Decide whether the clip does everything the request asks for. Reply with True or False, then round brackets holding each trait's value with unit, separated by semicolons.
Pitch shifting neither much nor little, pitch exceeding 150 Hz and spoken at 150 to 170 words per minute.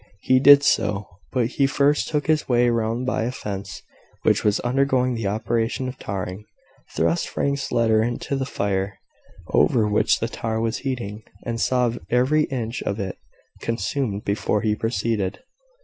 False (3.5 semitones; 115 Hz; 160 wpm)